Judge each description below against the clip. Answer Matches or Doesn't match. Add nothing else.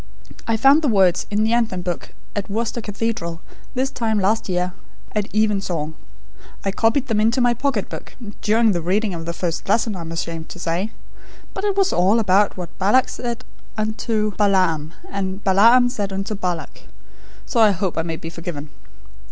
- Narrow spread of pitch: Doesn't match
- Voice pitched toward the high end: Matches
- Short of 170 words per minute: Doesn't match